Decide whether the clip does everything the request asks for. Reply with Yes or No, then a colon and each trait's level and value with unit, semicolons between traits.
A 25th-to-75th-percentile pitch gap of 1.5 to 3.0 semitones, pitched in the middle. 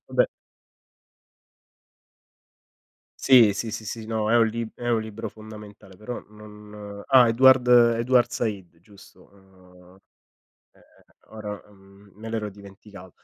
No: narrow, 2.5 semitones; low, 105 Hz